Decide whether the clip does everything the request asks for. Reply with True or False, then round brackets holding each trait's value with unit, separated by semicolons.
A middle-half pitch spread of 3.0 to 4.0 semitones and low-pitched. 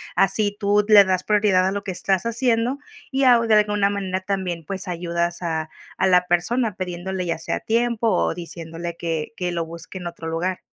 False (3.3 semitones; 185 Hz)